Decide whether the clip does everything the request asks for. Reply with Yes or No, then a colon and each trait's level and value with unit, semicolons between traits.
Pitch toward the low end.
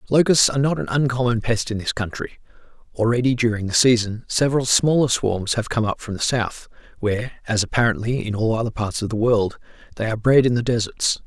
Yes: low, 115 Hz